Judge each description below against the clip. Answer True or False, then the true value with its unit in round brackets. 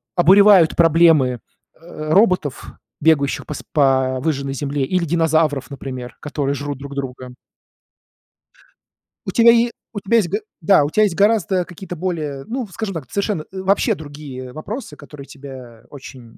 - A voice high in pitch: False (155 Hz)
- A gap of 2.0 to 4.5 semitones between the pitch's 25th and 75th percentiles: False (5.3 semitones)